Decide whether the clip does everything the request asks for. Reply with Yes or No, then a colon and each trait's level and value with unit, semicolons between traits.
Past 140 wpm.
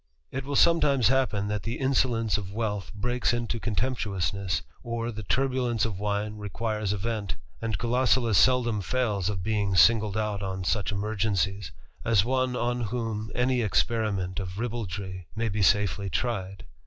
Yes: average, 155 wpm